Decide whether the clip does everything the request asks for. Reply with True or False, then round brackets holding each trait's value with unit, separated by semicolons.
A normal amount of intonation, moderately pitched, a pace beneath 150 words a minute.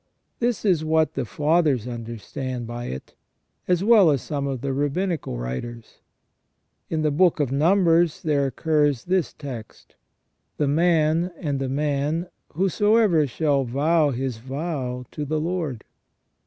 True (4.2 semitones; 150 Hz; 140 wpm)